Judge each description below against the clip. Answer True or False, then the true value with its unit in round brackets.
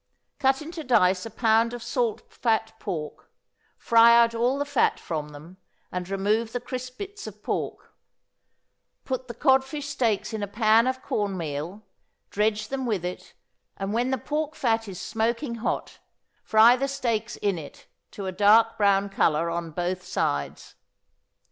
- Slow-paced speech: False (160 wpm)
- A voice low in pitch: False (225 Hz)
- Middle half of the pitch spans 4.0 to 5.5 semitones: True (4.4 semitones)